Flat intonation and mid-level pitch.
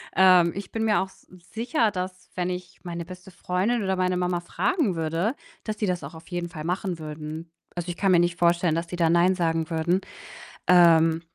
Yes: narrow, 2.0 semitones; medium, 180 Hz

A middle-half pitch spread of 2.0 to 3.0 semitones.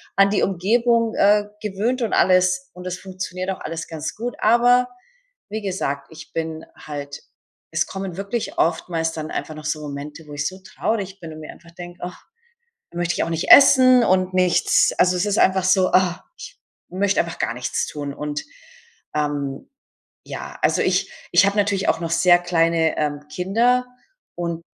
No: average, 3.8 semitones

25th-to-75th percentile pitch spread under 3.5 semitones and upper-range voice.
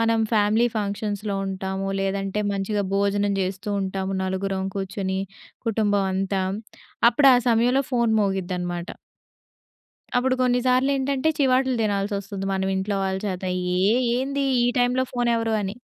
No: average, 3.8 semitones; high, 205 Hz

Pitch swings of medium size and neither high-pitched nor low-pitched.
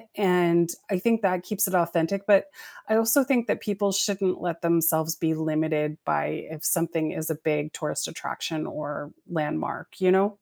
Yes: average, 3.7 semitones; medium, 170 Hz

